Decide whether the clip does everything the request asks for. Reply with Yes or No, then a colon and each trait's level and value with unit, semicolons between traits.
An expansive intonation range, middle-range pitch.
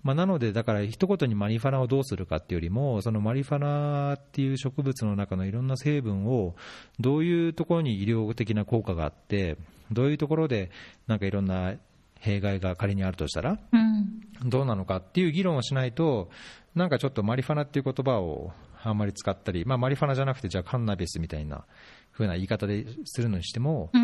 No: wide, 6.1 semitones; low, 115 Hz